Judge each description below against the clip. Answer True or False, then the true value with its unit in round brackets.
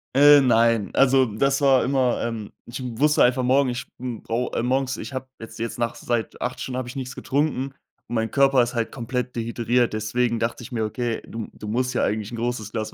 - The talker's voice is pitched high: False (120 Hz)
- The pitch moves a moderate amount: False (2.2 semitones)